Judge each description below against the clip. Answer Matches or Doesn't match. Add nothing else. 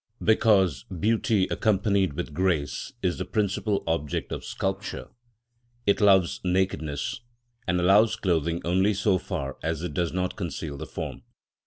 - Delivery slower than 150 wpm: Matches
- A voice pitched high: Doesn't match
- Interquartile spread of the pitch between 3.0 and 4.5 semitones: Matches